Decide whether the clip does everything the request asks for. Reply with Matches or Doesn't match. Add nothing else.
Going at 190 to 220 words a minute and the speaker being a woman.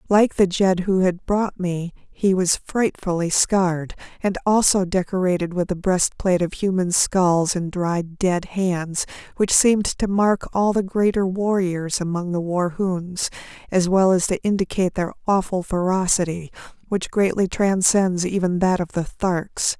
Doesn't match